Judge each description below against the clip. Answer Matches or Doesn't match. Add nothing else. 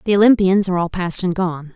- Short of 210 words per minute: Doesn't match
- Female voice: Matches